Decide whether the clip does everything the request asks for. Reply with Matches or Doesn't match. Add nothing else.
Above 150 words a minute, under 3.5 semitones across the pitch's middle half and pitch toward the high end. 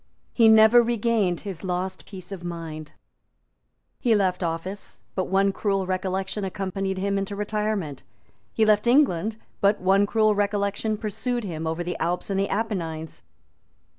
Doesn't match